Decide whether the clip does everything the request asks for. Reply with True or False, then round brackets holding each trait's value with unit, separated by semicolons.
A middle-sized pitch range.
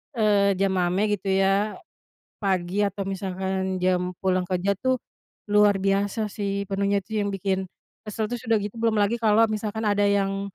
False (1.6 semitones)